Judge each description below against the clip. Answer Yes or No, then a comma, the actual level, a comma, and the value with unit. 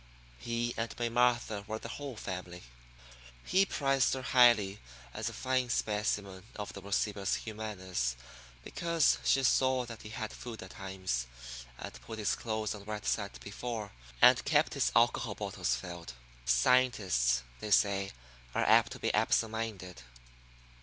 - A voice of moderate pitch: No, low, 105 Hz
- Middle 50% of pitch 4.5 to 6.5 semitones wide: No, average, 4.1 semitones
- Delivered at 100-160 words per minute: Yes, average, 150 wpm